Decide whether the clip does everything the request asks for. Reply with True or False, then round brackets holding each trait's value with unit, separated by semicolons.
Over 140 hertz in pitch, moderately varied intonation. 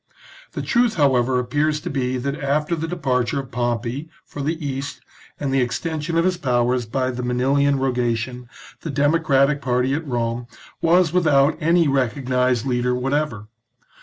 False (135 Hz; 3.4 semitones)